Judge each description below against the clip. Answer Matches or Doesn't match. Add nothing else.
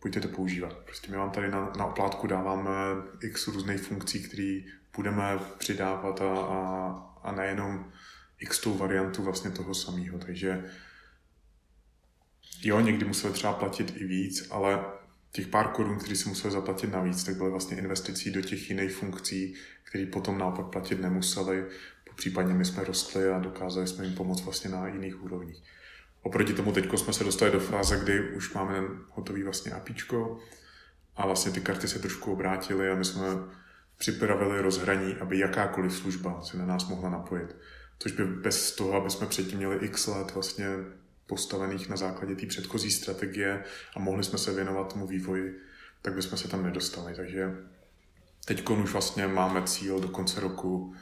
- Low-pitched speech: Matches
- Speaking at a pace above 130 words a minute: Matches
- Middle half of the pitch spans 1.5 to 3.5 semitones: Doesn't match